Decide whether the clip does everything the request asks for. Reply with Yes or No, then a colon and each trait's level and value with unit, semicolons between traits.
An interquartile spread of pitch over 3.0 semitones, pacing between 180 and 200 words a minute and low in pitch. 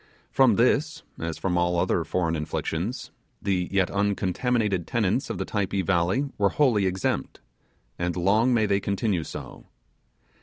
No: average, 4.5 semitones; average, 145 wpm; low, 100 Hz